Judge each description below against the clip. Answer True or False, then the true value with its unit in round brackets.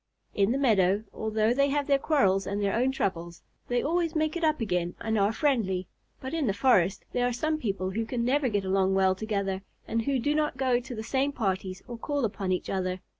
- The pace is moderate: False (225 wpm)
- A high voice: True (225 Hz)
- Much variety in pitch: True (5.9 semitones)